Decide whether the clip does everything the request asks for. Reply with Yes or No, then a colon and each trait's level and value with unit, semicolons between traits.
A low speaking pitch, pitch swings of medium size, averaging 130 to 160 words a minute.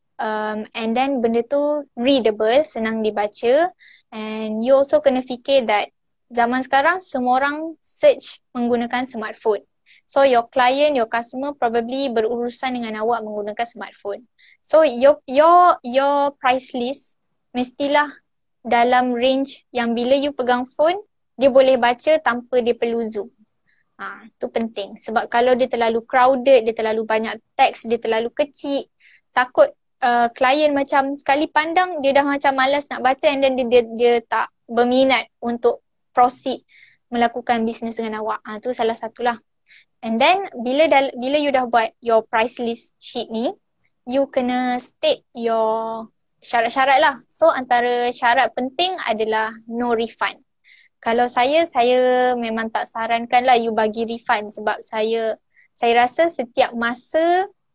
No: high, 245 Hz; average, 3.0 semitones; average, 145 wpm